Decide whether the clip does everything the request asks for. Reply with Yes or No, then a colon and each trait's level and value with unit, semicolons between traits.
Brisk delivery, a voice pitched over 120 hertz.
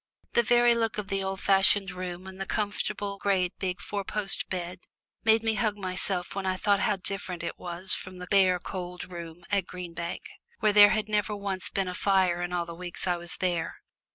Yes: fast, 210 wpm; high, 190 Hz